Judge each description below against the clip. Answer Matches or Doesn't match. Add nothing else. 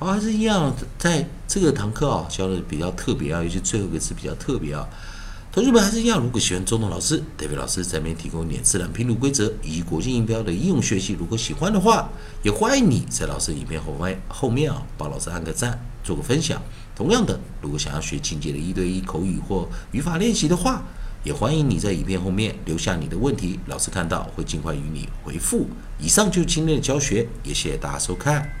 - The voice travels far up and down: Matches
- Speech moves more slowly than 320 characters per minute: Doesn't match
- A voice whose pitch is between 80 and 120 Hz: Matches